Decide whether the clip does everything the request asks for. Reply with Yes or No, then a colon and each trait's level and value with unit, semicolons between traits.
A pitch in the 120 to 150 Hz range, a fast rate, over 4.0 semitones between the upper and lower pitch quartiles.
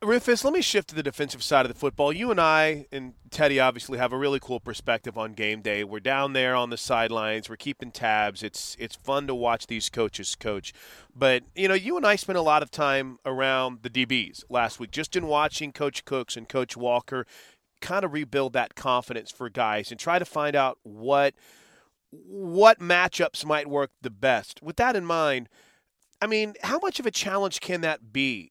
Yes: low, 135 Hz; fast, 210 wpm; average, 4.4 semitones